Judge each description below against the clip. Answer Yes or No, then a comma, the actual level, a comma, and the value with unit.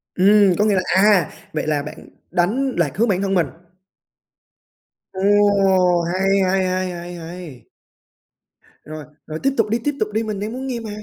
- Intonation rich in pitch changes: No, average, 3.6 semitones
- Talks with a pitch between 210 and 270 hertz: No, high, 190 Hz